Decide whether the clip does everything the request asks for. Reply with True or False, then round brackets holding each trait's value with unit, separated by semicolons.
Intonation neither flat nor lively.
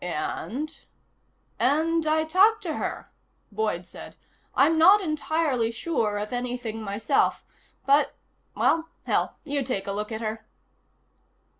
False (6.5 semitones)